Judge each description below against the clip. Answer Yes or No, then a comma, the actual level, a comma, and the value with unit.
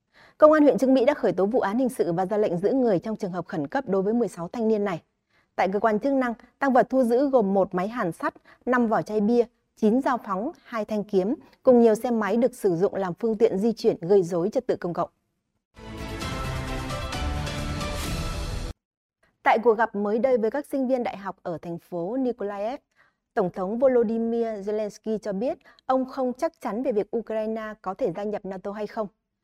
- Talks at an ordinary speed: Yes, average, 215 wpm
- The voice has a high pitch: Yes, high, 220 Hz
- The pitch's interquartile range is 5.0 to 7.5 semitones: No, average, 4.6 semitones